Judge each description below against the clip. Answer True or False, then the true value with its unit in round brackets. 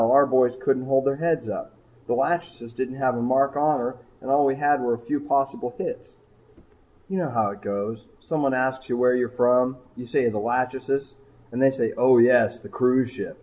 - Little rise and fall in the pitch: True (2.0 semitones)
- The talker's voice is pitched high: False (130 Hz)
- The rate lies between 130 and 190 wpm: False (205 wpm)